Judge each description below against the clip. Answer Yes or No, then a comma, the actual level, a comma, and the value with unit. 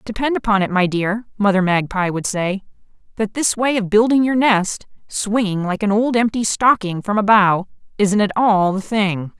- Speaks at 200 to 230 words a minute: No, average, 190 wpm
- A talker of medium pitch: No, high, 205 Hz